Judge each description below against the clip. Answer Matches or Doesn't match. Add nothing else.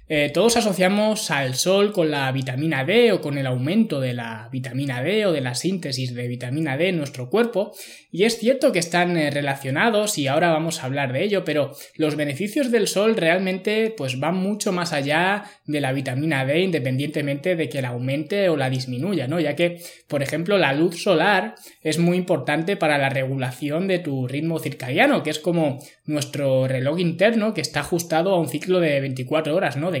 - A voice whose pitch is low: Doesn't match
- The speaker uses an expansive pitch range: Doesn't match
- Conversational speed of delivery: Doesn't match